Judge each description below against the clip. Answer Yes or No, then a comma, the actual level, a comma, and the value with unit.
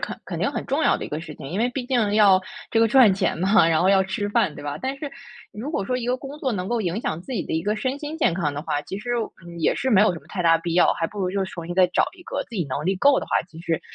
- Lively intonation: Yes, wide, 6.0 semitones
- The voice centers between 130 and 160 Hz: No, high, 195 Hz